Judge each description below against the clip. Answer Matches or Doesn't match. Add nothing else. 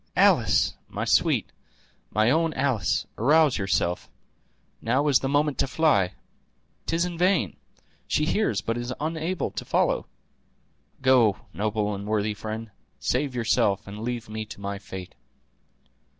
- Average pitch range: Doesn't match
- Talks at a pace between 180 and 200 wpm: Doesn't match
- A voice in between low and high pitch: Doesn't match